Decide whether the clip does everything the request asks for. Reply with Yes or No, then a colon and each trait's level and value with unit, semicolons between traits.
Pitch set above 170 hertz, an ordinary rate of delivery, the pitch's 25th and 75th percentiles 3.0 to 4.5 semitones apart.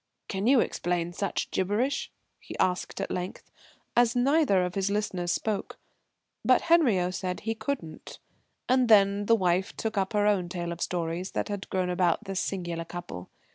Yes: high, 190 Hz; average, 170 wpm; average, 3.6 semitones